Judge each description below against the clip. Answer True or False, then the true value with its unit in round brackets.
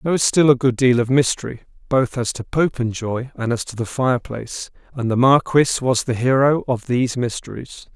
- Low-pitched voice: True (125 Hz)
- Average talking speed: True (195 wpm)